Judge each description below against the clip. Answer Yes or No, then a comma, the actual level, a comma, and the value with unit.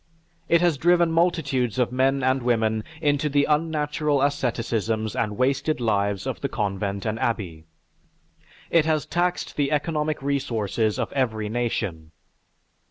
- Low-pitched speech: Yes, low, 130 Hz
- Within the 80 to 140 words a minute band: Yes, slow, 135 wpm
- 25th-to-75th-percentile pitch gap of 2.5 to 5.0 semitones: No, wide, 5.5 semitones